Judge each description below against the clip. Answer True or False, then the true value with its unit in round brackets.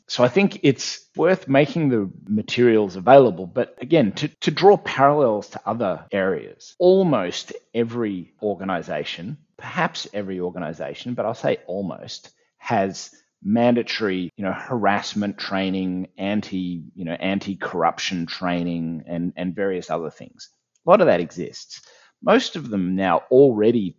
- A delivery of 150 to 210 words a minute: False (135 wpm)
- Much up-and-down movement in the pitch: True (6.8 semitones)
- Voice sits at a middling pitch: False (105 Hz)